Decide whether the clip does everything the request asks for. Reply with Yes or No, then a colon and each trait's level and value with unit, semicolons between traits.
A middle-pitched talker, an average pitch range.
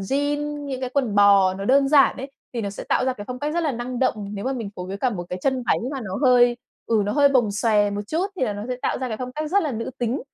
No: very high, 250 Hz; average, 5.0 semitones